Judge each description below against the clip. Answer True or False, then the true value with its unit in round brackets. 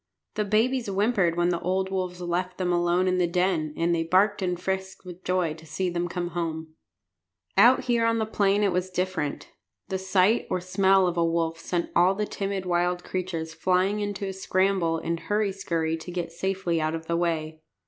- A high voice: False (180 Hz)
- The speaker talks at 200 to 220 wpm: True (205 wpm)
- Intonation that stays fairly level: True (2.3 semitones)